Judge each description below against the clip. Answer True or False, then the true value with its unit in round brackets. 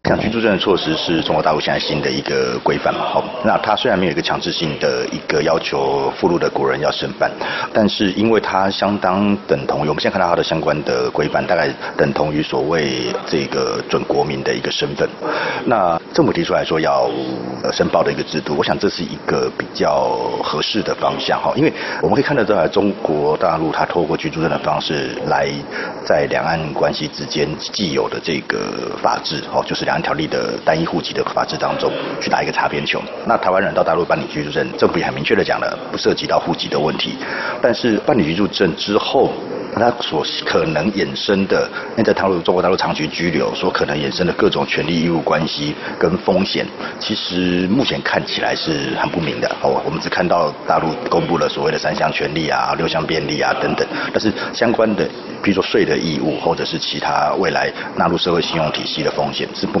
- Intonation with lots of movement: False (4.8 semitones)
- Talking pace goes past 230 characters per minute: True (325 characters per minute)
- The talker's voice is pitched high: False (90 Hz)